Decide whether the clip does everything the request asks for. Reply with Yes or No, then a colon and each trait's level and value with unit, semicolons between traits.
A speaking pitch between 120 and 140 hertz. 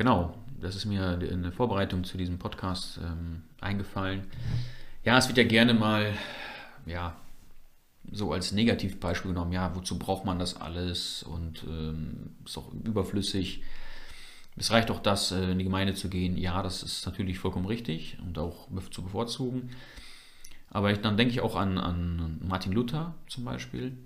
No: very low, 95 Hz